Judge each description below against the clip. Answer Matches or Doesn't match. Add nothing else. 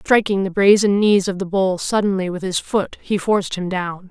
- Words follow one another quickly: Matches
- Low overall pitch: Doesn't match